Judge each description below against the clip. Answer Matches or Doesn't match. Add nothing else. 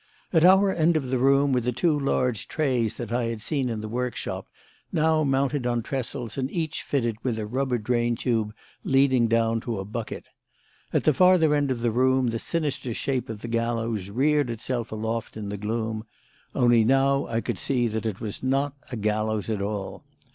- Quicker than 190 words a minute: Matches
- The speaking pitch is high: Doesn't match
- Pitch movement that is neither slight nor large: Matches